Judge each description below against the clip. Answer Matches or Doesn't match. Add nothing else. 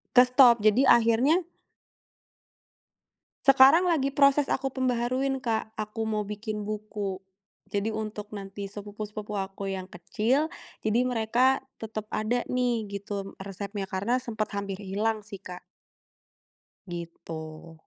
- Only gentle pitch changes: Doesn't match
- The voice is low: Doesn't match